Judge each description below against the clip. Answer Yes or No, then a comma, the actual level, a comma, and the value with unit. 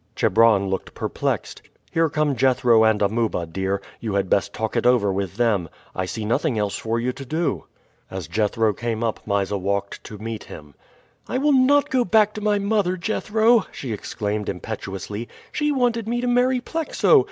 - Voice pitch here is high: No, low, 115 Hz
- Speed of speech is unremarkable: Yes, average, 180 wpm